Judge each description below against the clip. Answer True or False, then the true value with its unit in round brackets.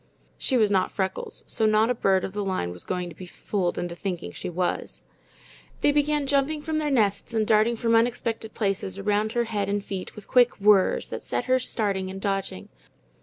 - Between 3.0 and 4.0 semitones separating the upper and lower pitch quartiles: True (3.6 semitones)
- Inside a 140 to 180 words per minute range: False (205 wpm)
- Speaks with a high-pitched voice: True (210 Hz)